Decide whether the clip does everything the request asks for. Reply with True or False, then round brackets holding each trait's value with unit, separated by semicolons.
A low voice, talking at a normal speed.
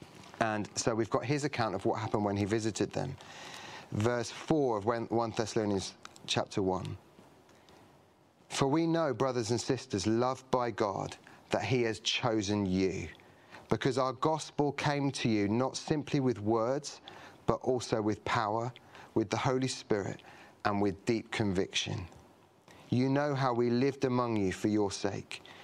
True (120 Hz; 155 wpm)